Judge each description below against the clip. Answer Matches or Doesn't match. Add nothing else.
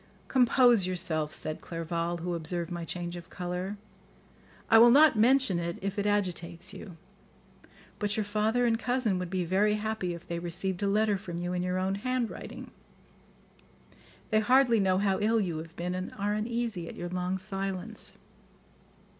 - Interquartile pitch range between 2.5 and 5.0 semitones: Matches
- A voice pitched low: Doesn't match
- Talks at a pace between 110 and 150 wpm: Doesn't match